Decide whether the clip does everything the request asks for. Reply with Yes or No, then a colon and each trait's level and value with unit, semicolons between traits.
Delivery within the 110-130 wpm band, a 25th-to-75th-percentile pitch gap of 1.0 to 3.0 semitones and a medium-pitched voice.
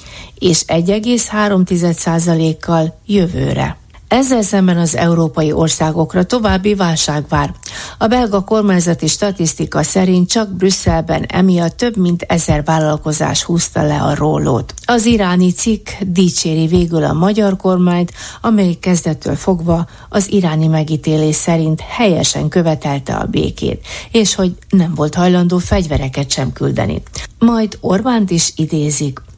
No: average, 120 wpm; average, 3.5 semitones; medium, 170 Hz